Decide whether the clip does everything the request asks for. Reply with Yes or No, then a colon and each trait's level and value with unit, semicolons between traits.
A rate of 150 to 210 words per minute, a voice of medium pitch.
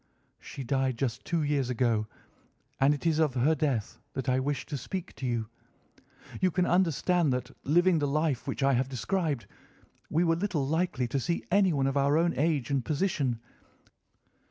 Yes: average, 180 wpm; medium, 145 Hz